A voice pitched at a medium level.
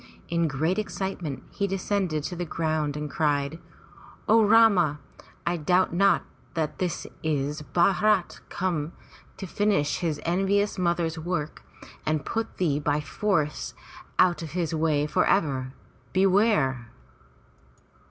Yes: medium, 170 Hz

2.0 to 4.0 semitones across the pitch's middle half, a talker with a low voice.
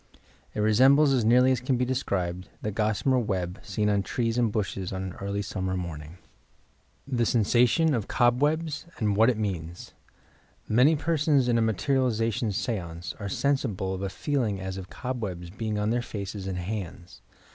No: average, 4.8 semitones; low, 110 Hz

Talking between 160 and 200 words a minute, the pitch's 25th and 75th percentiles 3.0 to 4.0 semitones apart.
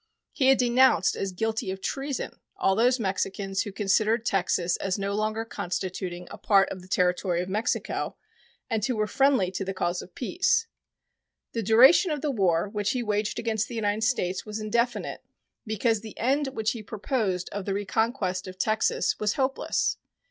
Yes: average, 175 wpm; average, 3.5 semitones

